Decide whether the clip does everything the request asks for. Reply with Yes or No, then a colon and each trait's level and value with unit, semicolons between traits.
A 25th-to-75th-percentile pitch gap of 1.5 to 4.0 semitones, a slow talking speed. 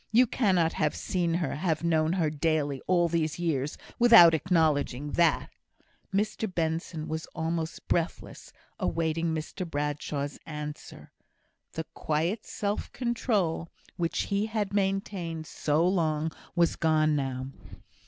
Yes: average, 3.0 semitones; slow, 125 wpm